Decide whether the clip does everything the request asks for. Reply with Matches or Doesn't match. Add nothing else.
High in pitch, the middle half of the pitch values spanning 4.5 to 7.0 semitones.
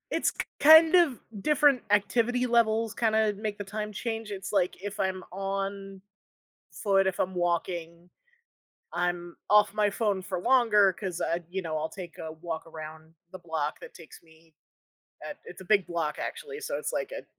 Doesn't match